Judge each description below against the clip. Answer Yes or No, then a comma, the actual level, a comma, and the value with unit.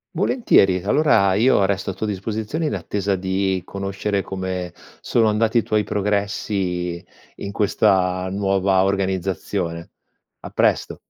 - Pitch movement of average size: No, narrow, 1.8 semitones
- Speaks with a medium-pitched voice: No, very low, 95 Hz